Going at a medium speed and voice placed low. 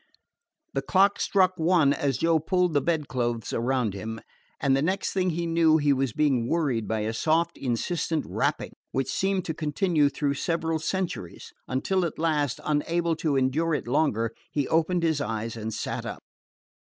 No: average, 165 wpm; medium, 150 Hz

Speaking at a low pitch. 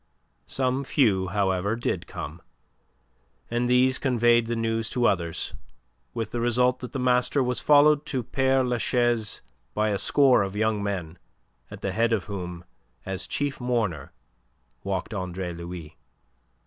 Yes: low, 115 Hz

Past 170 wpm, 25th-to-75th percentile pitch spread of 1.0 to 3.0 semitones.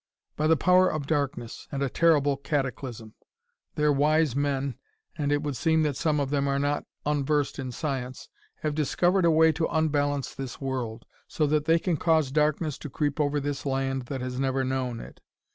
Yes: average, 190 wpm; narrow, 2.4 semitones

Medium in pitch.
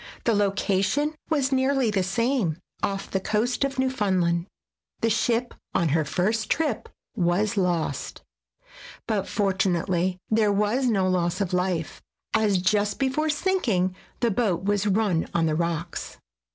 No: high, 200 Hz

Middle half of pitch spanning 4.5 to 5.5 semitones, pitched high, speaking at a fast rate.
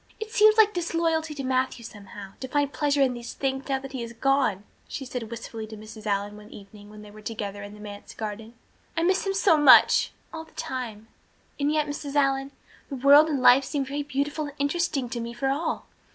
Yes: average, 5.1 semitones; very high, 270 Hz; fast, 220 wpm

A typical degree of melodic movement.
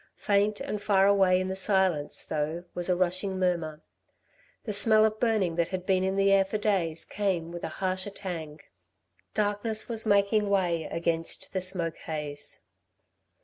Yes: average, 3.0 semitones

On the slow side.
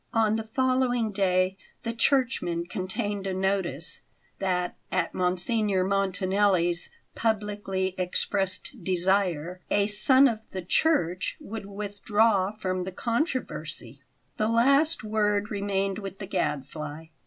Yes: slow, 115 wpm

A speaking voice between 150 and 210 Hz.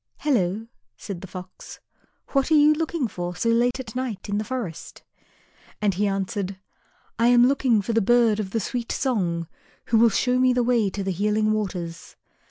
No: high, 220 Hz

